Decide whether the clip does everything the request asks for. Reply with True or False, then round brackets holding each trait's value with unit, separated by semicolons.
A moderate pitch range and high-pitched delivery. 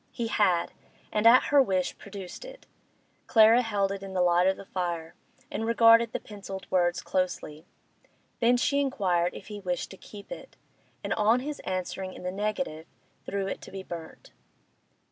True (3.9 semitones; 195 Hz)